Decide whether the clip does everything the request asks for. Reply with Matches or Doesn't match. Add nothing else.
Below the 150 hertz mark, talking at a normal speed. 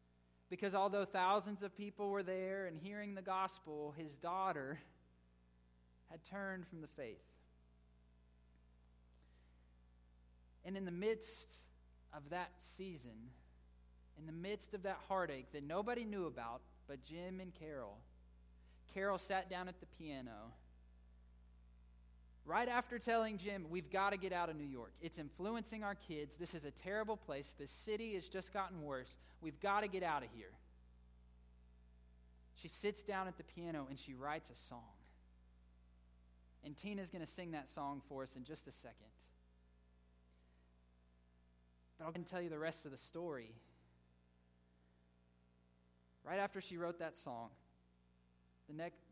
Matches